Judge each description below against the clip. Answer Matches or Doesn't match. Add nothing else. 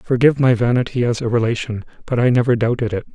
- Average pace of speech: Doesn't match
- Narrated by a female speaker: Doesn't match